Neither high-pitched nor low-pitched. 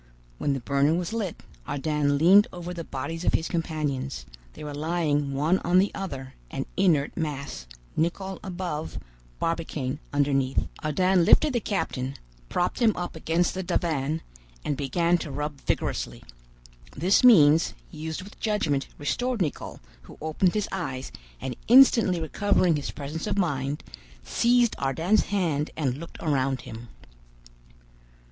Yes: medium, 160 Hz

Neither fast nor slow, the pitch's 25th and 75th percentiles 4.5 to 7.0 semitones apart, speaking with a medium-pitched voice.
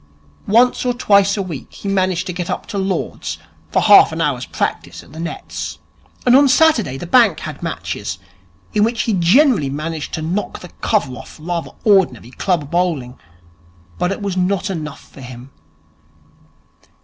Yes: average, 170 wpm; average, 5.0 semitones; medium, 180 Hz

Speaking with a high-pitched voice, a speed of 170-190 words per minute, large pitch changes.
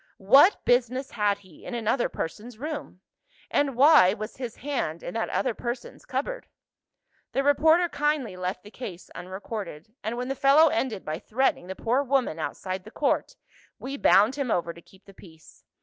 Yes: high, 235 Hz; average, 175 wpm; wide, 6.3 semitones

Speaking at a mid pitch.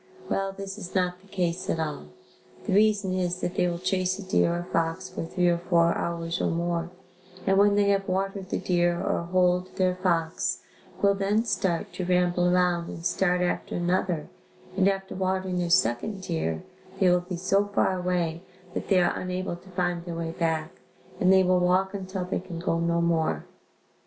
Yes: medium, 180 Hz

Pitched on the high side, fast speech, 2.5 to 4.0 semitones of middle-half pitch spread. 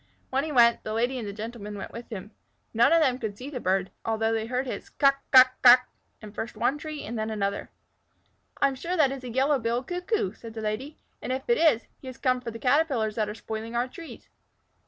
Yes: high, 240 Hz; fast, 240 wpm; average, 3.6 semitones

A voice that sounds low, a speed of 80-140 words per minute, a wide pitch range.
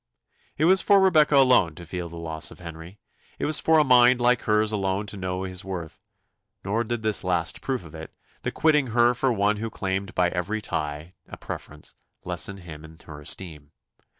No: very low, 95 Hz; average, 200 wpm; wide, 6.1 semitones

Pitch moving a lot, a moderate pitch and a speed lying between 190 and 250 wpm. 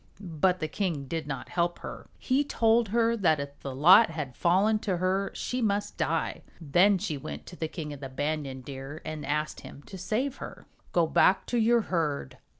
Yes: wide, 5.9 semitones; medium, 170 Hz; average, 200 wpm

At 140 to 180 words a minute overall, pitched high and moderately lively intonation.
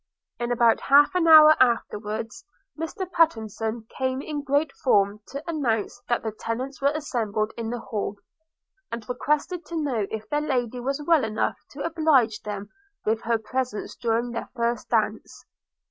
Yes: average, 160 wpm; high, 245 Hz; average, 4.8 semitones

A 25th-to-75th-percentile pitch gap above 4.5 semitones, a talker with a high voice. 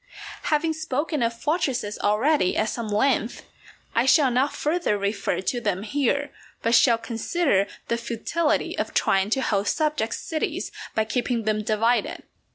Yes: average, 5.2 semitones; high, 235 Hz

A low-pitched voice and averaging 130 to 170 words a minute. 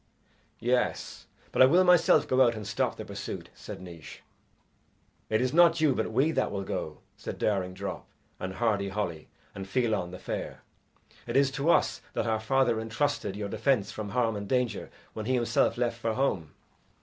No: low, 115 Hz; average, 185 wpm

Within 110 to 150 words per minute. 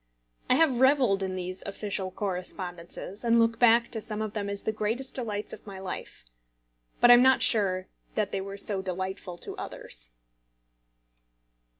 No: average, 170 wpm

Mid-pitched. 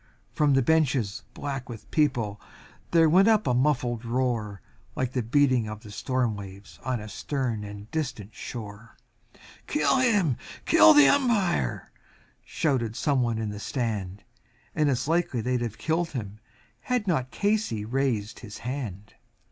No: low, 125 Hz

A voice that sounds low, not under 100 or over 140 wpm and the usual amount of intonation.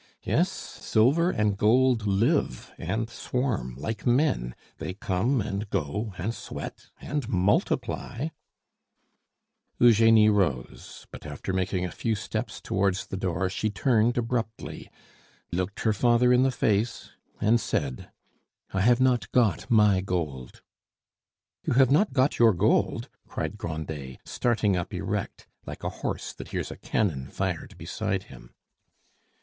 Yes: low, 105 Hz; slow, 135 wpm; average, 4.6 semitones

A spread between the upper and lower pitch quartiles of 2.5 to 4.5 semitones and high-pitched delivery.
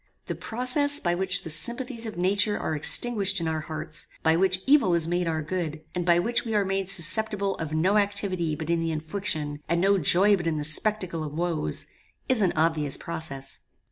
No: average, 4.2 semitones; medium, 175 Hz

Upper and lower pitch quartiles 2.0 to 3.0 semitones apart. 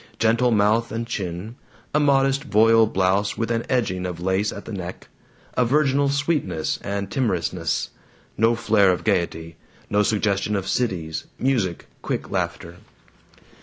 No: average, 4.3 semitones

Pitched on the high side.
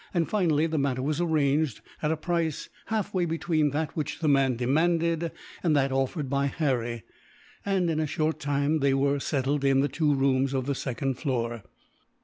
No: medium, 145 Hz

